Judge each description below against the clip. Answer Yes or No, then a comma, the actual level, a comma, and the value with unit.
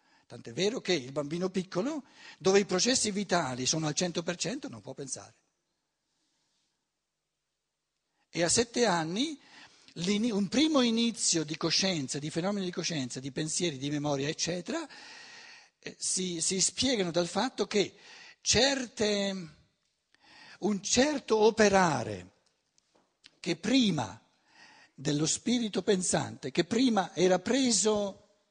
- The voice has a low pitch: No, high, 190 Hz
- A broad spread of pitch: Yes, wide, 5.9 semitones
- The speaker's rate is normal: No, slow, 110 wpm